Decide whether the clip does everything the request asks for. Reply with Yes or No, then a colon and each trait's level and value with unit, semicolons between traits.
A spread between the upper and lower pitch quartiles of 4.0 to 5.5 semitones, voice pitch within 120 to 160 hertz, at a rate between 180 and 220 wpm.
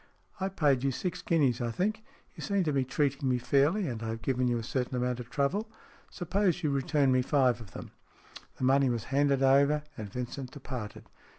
No: average, 3.3 semitones; low, 135 Hz; fast, 205 wpm